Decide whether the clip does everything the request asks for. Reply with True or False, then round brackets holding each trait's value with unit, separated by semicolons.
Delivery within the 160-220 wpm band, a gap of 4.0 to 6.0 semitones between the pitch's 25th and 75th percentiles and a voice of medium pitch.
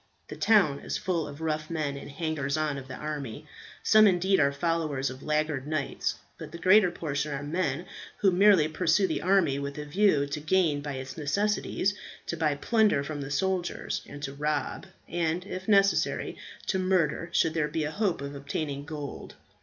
True (185 wpm; 4.3 semitones; 155 Hz)